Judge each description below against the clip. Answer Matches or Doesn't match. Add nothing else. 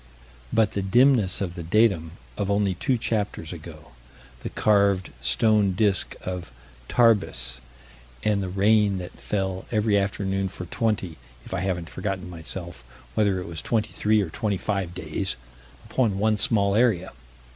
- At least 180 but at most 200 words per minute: Doesn't match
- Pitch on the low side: Matches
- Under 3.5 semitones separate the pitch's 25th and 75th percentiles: Matches